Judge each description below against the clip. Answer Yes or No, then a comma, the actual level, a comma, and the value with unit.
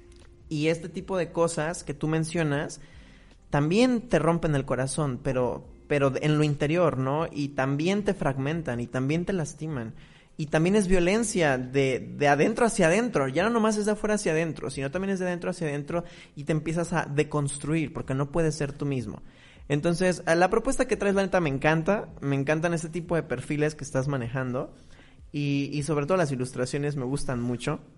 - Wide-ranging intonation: No, average, 3.8 semitones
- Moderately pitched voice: Yes, medium, 155 Hz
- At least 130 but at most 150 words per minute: No, fast, 190 wpm